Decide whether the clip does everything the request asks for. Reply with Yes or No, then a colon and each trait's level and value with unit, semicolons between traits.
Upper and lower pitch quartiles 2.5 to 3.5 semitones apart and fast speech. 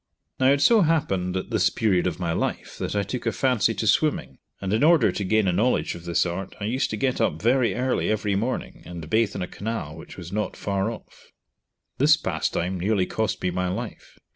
No: average, 5.1 semitones; fast, 220 wpm